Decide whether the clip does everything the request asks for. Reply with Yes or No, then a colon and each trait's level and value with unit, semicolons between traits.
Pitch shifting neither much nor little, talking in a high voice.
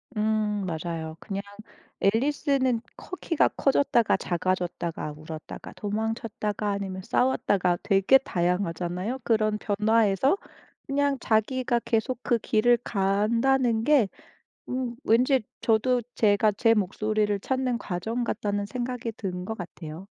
Yes: average, 3.9 semitones; high, 215 Hz